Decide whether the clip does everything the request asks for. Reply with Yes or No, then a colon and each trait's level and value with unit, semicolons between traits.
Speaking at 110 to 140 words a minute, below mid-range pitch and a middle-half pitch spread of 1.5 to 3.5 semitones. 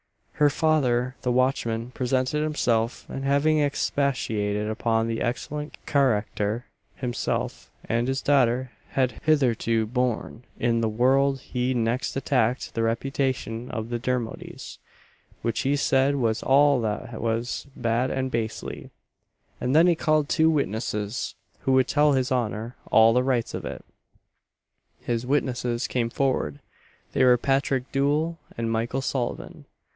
Yes: slow, 135 wpm; low, 125 Hz; average, 3.0 semitones